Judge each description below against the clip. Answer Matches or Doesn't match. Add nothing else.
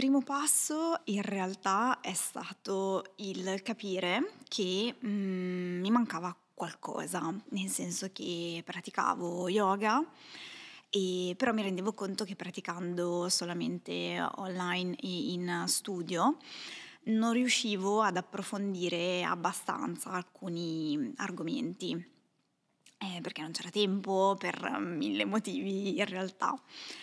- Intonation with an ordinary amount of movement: Matches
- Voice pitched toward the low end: Doesn't match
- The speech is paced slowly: Matches